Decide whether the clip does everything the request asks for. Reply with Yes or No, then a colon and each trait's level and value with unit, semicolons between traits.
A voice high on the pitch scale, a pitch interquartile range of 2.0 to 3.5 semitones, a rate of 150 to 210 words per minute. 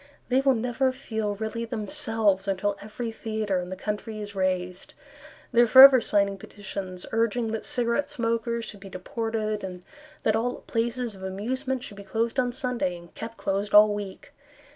Yes: high, 220 Hz; average, 3.0 semitones; average, 170 wpm